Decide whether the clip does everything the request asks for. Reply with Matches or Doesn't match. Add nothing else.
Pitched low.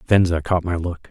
Matches